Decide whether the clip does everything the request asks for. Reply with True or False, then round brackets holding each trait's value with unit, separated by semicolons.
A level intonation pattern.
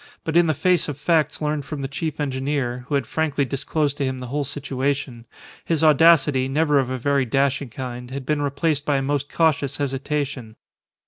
True (2.2 semitones)